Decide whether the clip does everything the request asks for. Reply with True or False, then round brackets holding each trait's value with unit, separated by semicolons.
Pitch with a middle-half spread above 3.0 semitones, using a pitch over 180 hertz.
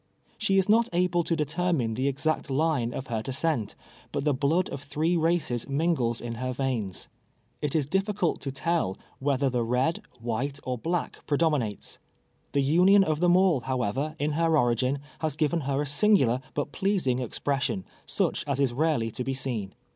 False (4.5 semitones; 140 Hz)